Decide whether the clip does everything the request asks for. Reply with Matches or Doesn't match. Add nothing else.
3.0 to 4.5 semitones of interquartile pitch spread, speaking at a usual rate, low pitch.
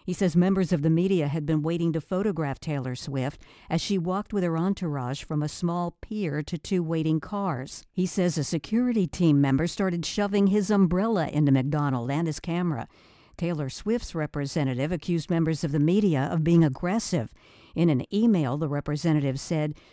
Doesn't match